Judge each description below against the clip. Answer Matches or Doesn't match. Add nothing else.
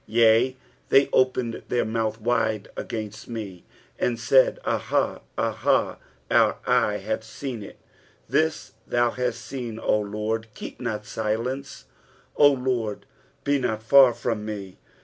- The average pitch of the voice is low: Matches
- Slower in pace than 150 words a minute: Matches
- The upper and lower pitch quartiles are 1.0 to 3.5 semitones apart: Matches